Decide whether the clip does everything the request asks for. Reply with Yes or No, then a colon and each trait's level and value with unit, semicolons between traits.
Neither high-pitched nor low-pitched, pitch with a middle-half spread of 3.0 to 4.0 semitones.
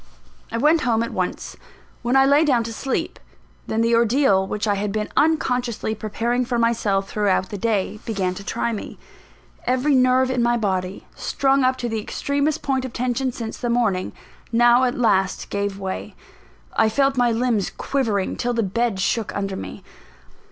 No: high, 235 Hz; average, 3.7 semitones